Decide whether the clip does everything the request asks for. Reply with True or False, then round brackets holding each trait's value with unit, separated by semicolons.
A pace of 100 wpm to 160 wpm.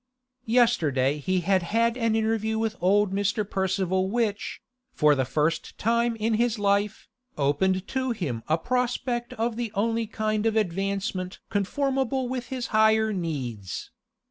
True (145 wpm)